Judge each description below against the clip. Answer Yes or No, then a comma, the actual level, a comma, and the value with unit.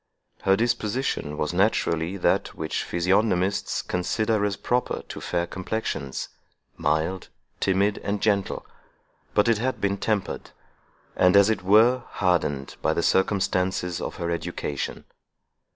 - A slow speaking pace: Yes, slow, 125 wpm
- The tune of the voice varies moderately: Yes, average, 3.3 semitones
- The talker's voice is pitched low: Yes, very low, 95 Hz